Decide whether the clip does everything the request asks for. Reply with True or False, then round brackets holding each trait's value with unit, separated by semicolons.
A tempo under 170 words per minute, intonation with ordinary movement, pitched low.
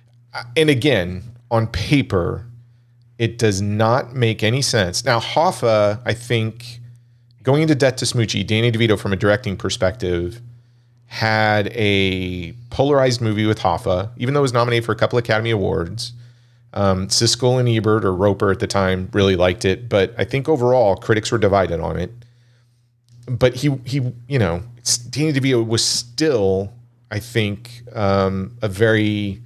True (155 wpm; 3.0 semitones; 115 Hz)